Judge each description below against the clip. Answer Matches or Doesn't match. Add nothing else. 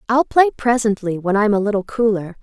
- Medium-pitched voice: Doesn't match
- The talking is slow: Doesn't match